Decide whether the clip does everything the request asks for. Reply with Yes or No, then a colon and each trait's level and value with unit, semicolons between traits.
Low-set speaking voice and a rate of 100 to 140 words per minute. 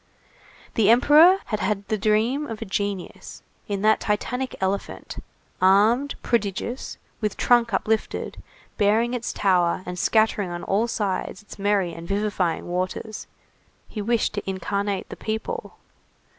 No: high, 210 Hz; slow, 135 wpm